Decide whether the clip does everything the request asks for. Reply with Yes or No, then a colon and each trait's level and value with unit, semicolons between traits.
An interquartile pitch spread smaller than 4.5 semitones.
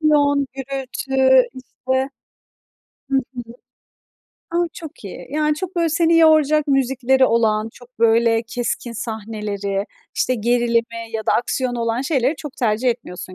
Yes: average, 3.3 semitones